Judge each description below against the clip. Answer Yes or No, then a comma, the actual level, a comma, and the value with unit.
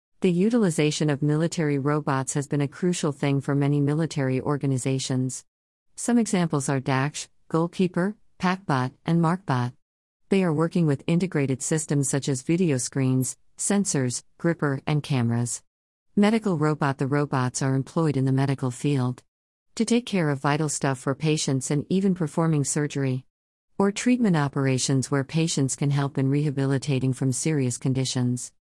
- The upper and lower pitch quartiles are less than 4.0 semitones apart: Yes, average, 3.6 semitones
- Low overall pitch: No, medium, 145 Hz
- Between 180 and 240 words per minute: No, average, 145 wpm